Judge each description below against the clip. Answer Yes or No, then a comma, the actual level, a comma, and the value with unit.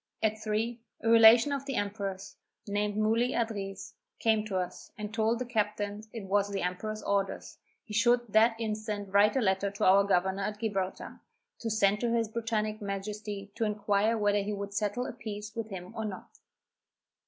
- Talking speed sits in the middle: Yes, average, 180 wpm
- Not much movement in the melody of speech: Yes, narrow, 2.0 semitones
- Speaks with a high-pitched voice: Yes, high, 210 Hz